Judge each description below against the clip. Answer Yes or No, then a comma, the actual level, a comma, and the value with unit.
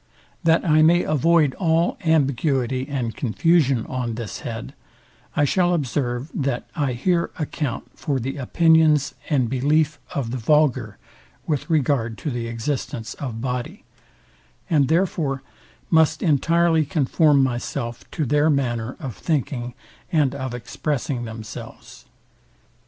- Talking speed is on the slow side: Yes, slow, 125 wpm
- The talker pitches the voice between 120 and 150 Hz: Yes, medium, 140 Hz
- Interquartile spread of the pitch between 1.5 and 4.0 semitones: No, average, 4.4 semitones